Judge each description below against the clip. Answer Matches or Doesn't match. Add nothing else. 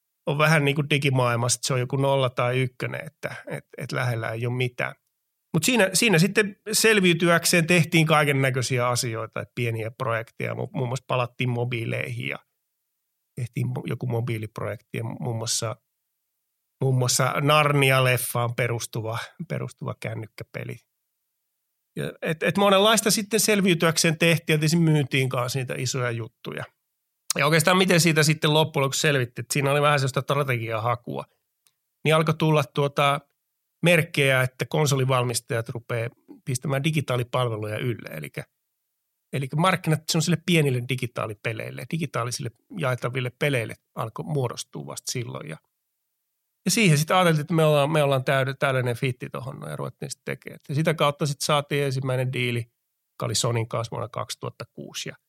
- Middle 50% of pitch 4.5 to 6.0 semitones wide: Doesn't match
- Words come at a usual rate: Matches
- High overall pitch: Doesn't match